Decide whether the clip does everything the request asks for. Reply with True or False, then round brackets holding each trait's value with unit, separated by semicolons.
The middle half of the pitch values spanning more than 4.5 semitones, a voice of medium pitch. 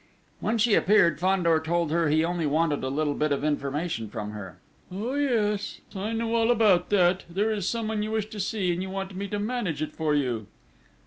True (5.6 semitones; 180 Hz)